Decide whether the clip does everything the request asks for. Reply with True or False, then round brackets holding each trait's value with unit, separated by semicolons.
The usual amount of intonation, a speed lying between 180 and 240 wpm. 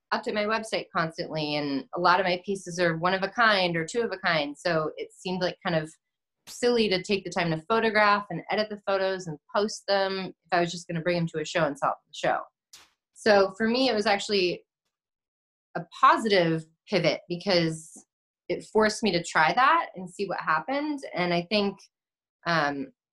True (3.8 semitones; 205 wpm)